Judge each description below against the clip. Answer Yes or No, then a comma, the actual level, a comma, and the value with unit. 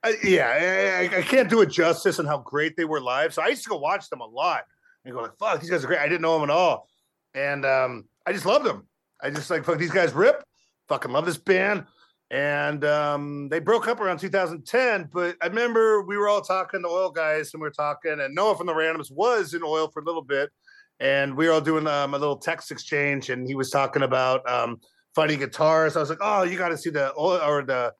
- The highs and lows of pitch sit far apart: No, average, 4.3 semitones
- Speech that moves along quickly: Yes, fast, 255 wpm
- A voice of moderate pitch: Yes, medium, 160 Hz